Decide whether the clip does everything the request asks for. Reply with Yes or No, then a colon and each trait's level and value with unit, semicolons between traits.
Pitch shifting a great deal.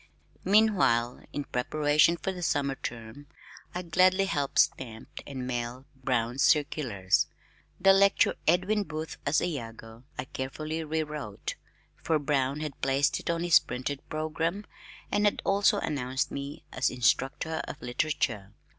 No: average, 4.7 semitones